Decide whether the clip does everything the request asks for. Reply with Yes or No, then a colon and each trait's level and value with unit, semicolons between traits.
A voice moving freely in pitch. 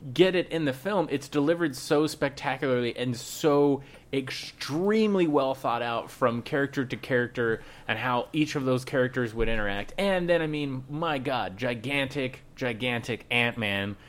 No: average, 3.6 semitones